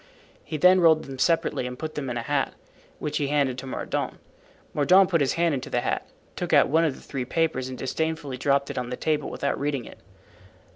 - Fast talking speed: Yes, fast, 225 wpm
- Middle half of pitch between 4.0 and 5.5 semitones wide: No, average, 3.4 semitones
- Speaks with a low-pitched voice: No, medium, 145 Hz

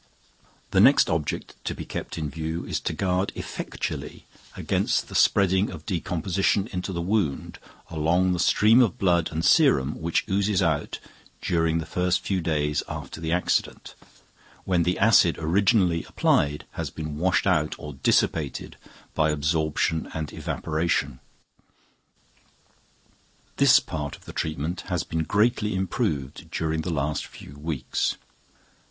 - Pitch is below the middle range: Yes, very low, 85 Hz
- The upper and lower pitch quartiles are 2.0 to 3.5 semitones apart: Yes, average, 3.2 semitones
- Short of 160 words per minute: Yes, average, 140 wpm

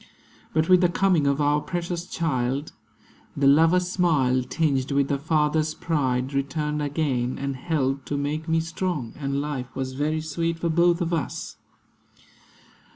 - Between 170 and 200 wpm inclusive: No, average, 155 wpm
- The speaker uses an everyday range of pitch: Yes, average, 3.2 semitones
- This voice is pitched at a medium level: Yes, medium, 150 Hz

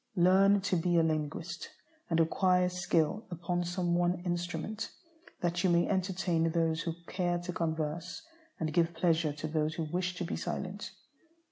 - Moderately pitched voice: Yes, medium, 175 Hz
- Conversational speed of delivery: Yes, average, 160 wpm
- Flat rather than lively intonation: Yes, narrow, 1.8 semitones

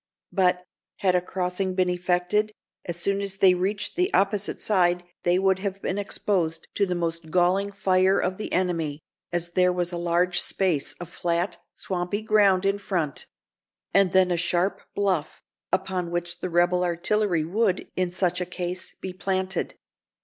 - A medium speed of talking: Yes, average, 165 wpm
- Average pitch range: No, narrow, 1.8 semitones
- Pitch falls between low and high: Yes, medium, 180 Hz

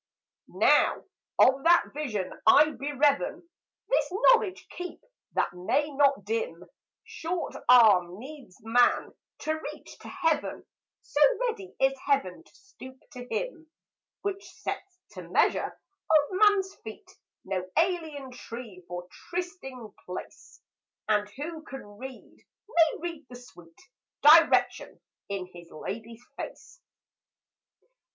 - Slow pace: Yes, slow, 115 wpm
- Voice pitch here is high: Yes, very high, 280 Hz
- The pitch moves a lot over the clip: Yes, wide, 7.4 semitones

